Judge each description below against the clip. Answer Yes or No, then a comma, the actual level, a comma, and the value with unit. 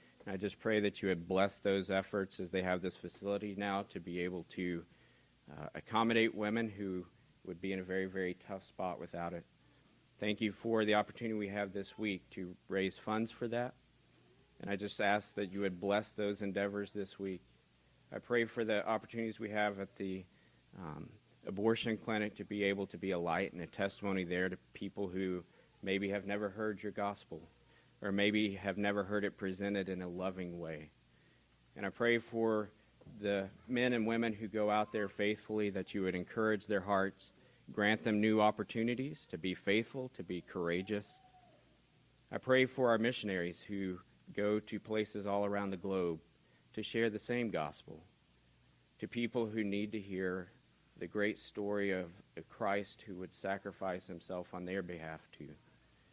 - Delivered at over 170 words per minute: Yes, average, 180 wpm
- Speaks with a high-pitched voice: No, low, 100 Hz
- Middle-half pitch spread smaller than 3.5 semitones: Yes, narrow, 2.4 semitones